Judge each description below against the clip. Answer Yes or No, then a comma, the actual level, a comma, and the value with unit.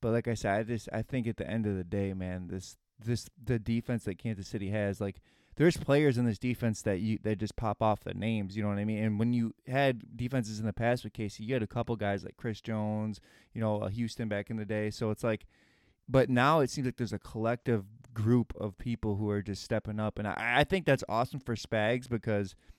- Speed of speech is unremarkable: No, fast, 255 wpm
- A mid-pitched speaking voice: No, low, 110 Hz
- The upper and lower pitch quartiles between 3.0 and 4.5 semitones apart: No, narrow, 2.5 semitones